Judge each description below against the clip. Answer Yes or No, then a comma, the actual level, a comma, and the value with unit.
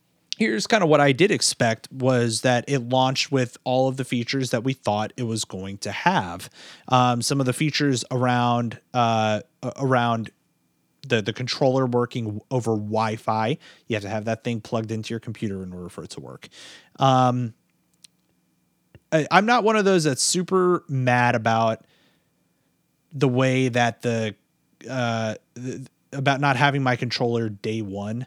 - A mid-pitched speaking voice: No, low, 125 Hz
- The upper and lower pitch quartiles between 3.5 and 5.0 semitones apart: No, average, 3.0 semitones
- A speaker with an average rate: Yes, average, 165 wpm